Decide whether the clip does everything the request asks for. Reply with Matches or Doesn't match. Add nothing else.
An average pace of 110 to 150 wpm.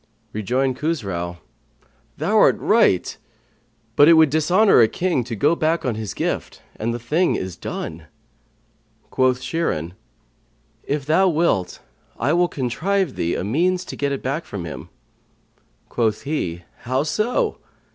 Matches